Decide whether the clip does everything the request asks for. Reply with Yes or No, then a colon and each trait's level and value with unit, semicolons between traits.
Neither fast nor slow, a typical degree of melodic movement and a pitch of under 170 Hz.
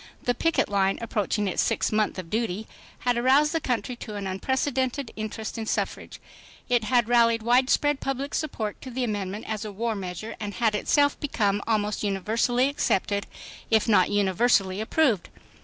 No: average, 170 wpm; average, 3.5 semitones; high, 225 Hz